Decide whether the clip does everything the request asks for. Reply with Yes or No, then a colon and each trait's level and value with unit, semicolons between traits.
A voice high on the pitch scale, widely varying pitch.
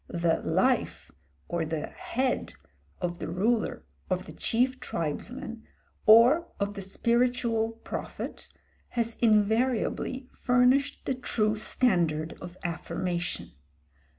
Yes: high, 220 Hz; wide, 5.9 semitones